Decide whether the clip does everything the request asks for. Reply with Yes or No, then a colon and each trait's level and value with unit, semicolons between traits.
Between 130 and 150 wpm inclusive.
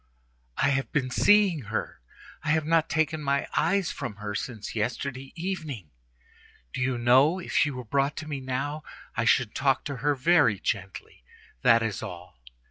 No: average, 170 wpm